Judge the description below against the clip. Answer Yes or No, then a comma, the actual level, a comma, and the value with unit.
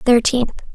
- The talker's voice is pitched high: Yes, high, 240 Hz